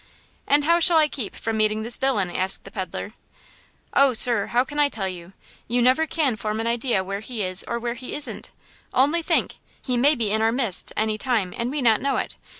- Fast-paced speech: Yes, fast, 225 wpm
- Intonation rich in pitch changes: No, average, 4.2 semitones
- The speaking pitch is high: Yes, high, 235 Hz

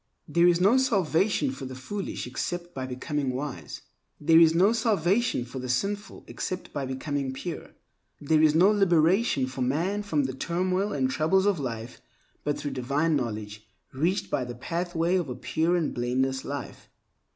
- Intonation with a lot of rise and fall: Yes, wide, 5.8 semitones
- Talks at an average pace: Yes, average, 170 wpm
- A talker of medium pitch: Yes, medium, 155 Hz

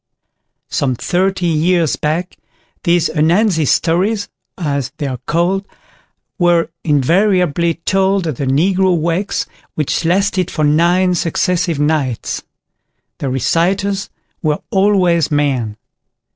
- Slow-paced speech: Yes, slow, 105 wpm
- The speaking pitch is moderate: Yes, medium, 170 Hz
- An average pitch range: Yes, average, 3.7 semitones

